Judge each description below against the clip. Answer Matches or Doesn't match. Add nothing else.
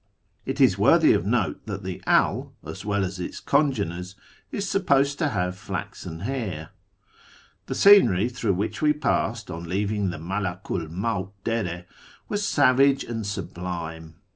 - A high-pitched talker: Doesn't match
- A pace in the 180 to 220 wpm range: Doesn't match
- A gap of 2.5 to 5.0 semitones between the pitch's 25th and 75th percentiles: Doesn't match